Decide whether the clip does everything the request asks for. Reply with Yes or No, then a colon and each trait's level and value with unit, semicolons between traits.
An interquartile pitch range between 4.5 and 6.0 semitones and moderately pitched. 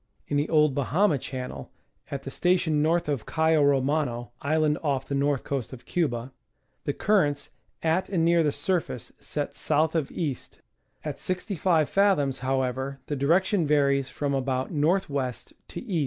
No: average, 3.4 semitones; medium, 145 Hz